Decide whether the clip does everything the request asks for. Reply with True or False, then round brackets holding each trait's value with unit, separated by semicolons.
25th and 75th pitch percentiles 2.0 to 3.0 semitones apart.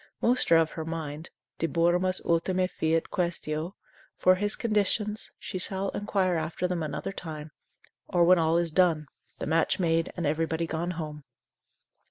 True (2.4 semitones)